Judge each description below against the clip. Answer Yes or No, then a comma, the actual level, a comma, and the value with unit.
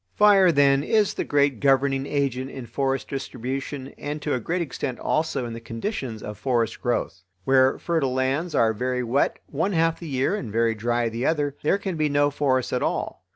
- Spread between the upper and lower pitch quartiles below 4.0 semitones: Yes, average, 3.5 semitones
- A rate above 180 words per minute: Yes, average, 200 wpm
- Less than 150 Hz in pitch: Yes, low, 135 Hz